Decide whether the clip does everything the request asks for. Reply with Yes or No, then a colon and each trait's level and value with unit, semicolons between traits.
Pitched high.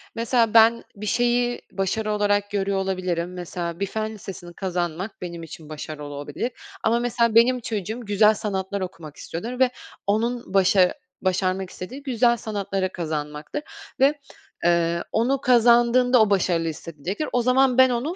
Yes: high, 205 Hz